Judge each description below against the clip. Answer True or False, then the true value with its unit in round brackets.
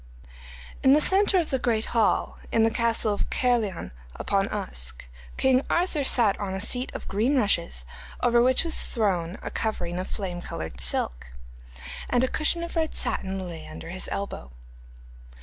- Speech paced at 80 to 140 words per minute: False (165 wpm)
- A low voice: False (220 Hz)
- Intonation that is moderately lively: False (6.4 semitones)